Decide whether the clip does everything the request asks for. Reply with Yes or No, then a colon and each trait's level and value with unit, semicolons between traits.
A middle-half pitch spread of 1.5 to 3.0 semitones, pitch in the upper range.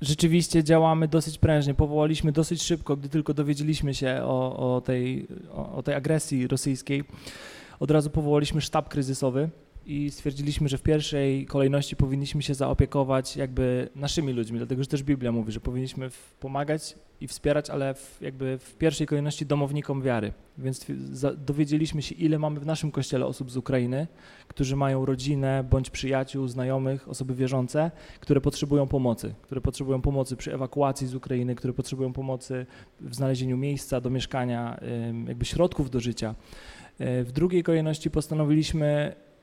No: narrow, 2.5 semitones; medium, 140 Hz